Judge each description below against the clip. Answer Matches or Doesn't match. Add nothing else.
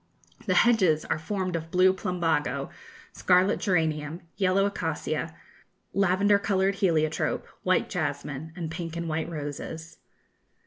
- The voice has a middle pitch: Matches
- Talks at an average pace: Doesn't match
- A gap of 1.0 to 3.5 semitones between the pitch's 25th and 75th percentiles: Matches